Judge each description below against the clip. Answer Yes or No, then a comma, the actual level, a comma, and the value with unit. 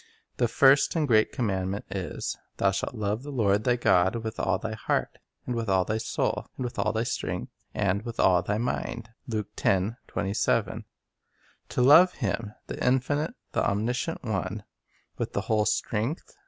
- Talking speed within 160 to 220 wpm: Yes, average, 170 wpm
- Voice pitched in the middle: No, low, 110 Hz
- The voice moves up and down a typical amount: Yes, average, 3.5 semitones